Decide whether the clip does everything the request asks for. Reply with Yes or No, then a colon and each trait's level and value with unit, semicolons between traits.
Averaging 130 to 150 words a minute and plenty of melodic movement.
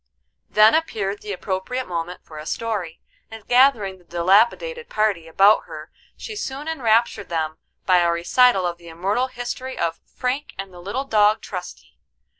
No: average, 160 wpm; wide, 6.0 semitones